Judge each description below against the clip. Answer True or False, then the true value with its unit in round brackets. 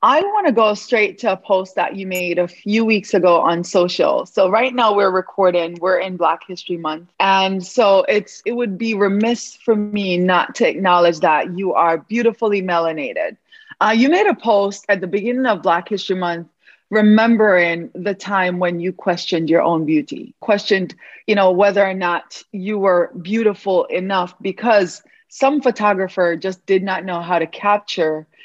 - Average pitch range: True (3.4 semitones)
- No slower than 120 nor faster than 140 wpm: False (180 wpm)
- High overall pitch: True (195 Hz)